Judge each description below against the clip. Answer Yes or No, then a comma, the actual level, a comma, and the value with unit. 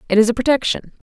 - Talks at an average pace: No, fast, 225 wpm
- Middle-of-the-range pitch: No, high, 240 Hz